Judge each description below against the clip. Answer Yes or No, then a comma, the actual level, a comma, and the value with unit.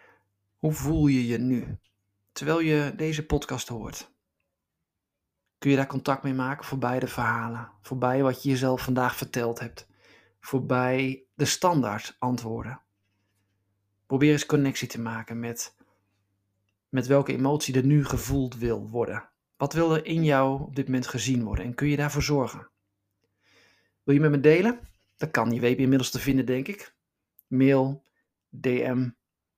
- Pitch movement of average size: Yes, average, 4.1 semitones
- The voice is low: Yes, low, 130 Hz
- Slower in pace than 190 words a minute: Yes, average, 155 wpm